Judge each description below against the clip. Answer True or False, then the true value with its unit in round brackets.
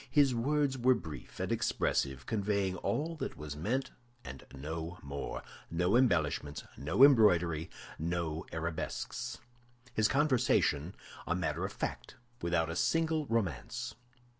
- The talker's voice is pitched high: False (90 Hz)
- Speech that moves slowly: True (130 wpm)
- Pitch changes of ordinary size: False (8.2 semitones)